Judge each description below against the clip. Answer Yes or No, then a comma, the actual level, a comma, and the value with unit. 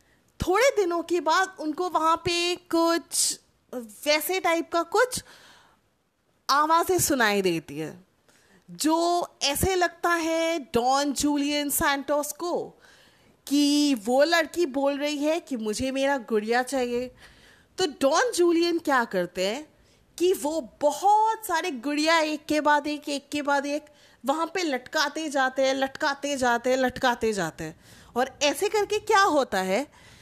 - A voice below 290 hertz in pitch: No, very high, 295 Hz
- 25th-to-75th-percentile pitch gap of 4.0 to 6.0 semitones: Yes, average, 4.4 semitones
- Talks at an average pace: Yes, average, 140 wpm